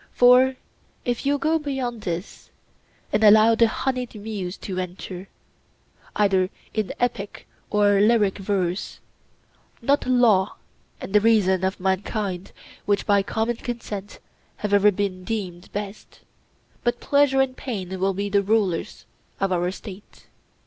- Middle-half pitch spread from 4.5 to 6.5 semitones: No, average, 3.7 semitones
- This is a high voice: Yes, high, 205 Hz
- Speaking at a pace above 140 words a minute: No, slow, 135 wpm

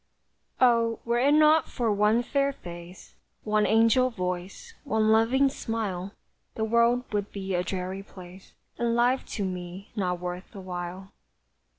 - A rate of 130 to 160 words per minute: Yes, average, 150 wpm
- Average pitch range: Yes, average, 4.4 semitones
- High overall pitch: Yes, high, 215 Hz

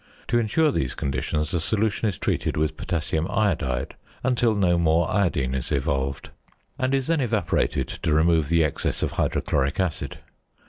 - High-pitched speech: No, very low, 85 Hz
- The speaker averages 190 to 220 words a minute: No, average, 155 wpm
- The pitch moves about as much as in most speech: No, wide, 6.2 semitones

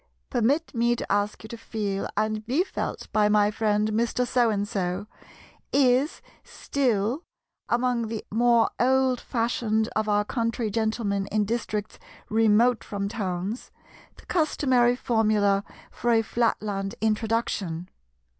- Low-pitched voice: No, high, 220 Hz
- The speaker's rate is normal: No, slow, 125 wpm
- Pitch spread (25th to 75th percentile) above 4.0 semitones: No, narrow, 2.5 semitones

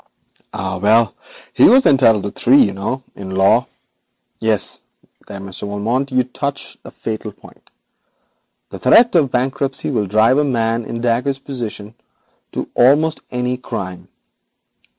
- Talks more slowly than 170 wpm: Yes, average, 140 wpm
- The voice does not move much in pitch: No, average, 4.3 semitones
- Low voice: Yes, low, 120 Hz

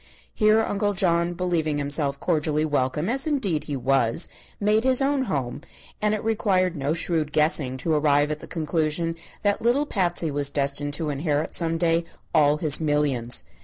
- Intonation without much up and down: No, average, 4.7 semitones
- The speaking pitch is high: No, medium, 160 Hz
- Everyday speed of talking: Yes, average, 165 wpm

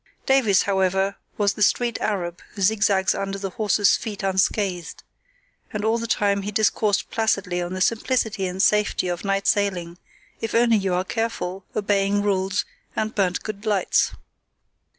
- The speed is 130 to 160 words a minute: Yes, average, 155 wpm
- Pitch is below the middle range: No, high, 200 Hz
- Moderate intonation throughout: No, narrow, 2.1 semitones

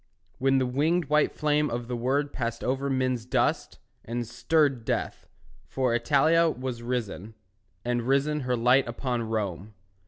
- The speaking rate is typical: Yes, average, 150 wpm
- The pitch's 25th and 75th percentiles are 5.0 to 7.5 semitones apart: No, average, 2.9 semitones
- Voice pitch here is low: Yes, low, 125 Hz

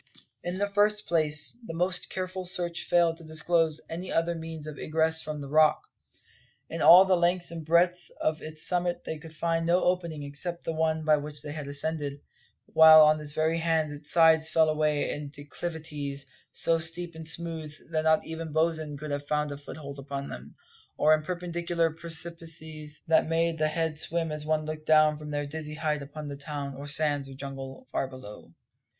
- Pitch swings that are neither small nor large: No, narrow, 1.9 semitones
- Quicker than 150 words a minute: Yes, average, 190 wpm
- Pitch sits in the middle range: Yes, medium, 155 Hz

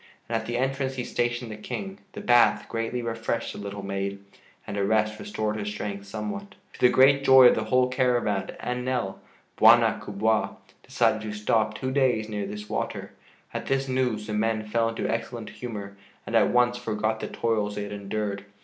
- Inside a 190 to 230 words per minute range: Yes, average, 195 wpm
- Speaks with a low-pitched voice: Yes, low, 110 Hz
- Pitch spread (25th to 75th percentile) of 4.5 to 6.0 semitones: No, average, 2.9 semitones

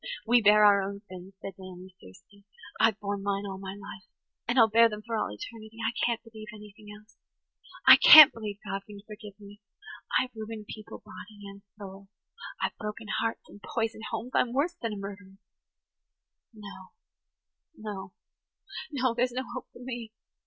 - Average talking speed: Yes, average, 160 wpm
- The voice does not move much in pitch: Yes, narrow, 2.3 semitones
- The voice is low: No, high, 210 Hz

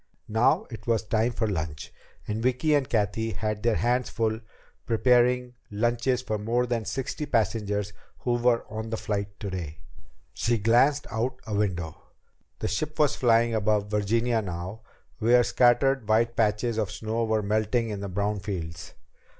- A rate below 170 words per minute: Yes, average, 160 wpm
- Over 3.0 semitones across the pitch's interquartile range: No, average, 2.7 semitones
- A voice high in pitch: No, low, 110 Hz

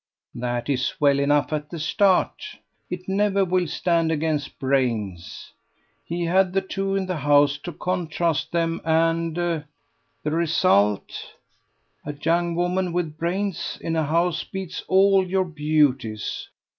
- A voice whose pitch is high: No, medium, 165 Hz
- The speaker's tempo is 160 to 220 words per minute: No, slow, 135 wpm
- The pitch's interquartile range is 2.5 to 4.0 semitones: Yes, average, 3.6 semitones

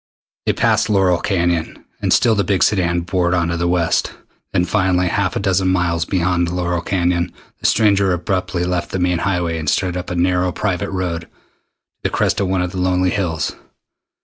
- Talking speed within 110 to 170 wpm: No, average, 195 wpm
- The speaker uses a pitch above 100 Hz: No, very low, 90 Hz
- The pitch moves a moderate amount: No, narrow, 1.4 semitones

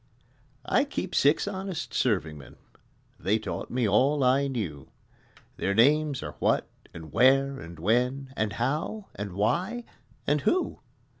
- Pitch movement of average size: No, wide, 6.2 semitones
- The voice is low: Yes, low, 130 Hz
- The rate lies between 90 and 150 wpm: Yes, average, 140 wpm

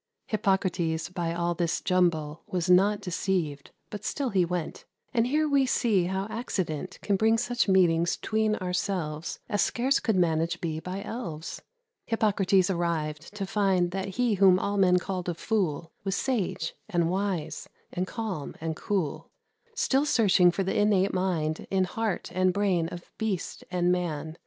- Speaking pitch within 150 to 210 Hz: Yes, medium, 185 Hz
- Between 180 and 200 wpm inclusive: No, average, 160 wpm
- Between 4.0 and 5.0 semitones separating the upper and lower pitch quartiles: No, average, 3.3 semitones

